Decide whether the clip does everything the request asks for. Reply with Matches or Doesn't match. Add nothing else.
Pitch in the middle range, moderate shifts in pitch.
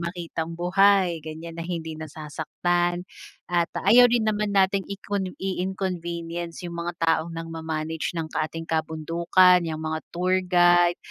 Doesn't match